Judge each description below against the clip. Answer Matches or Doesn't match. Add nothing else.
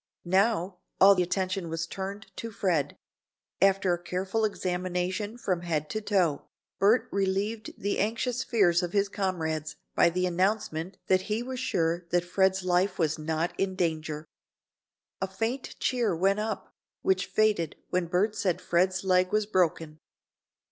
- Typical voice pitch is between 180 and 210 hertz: Matches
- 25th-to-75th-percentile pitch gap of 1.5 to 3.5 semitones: Matches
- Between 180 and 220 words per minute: Doesn't match